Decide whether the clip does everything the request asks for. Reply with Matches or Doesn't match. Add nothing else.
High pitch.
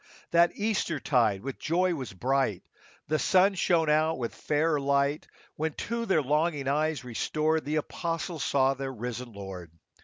Doesn't match